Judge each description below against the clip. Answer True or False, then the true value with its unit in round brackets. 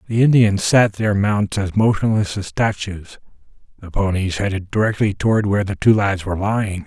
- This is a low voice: True (100 Hz)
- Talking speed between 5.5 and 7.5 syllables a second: False (5.3 syllables/s)